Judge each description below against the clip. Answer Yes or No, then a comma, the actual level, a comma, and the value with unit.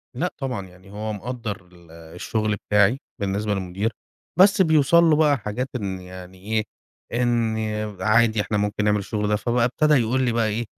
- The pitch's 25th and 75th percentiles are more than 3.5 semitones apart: Yes, average, 3.9 semitones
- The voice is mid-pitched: No, low, 110 Hz